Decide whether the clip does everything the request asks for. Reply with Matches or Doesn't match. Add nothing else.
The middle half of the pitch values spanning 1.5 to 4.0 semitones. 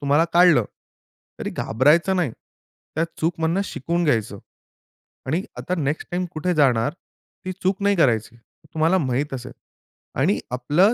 Doesn't match